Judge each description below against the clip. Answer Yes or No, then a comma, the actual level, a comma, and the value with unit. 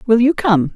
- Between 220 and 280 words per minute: Yes, fast, 240 wpm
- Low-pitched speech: No, high, 225 Hz